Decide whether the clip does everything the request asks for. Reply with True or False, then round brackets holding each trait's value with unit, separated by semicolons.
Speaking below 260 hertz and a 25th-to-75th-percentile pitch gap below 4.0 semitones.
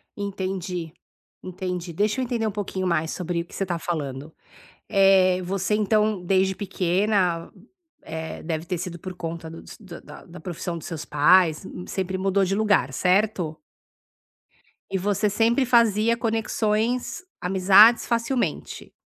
True (190 Hz; 3.4 semitones)